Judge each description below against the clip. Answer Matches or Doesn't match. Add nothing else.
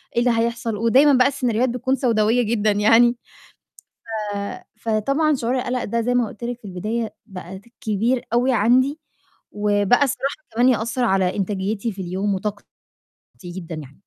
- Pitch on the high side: Matches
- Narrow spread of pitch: Doesn't match